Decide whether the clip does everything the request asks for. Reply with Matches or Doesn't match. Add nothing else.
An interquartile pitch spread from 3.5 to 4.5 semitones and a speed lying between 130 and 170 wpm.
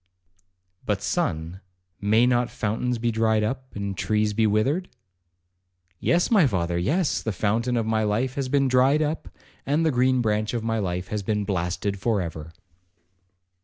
Matches